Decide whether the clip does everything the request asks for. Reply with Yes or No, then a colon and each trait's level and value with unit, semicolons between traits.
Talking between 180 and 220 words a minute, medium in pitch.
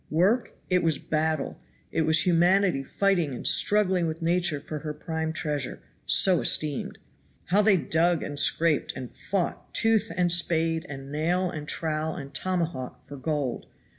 No: average, 155 wpm; medium, 160 Hz